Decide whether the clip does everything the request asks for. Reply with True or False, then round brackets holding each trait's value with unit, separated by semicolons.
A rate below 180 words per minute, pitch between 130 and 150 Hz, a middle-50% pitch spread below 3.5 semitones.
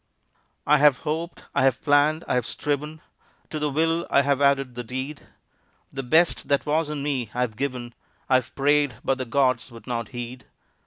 False (190 wpm; 140 Hz; 3.0 semitones)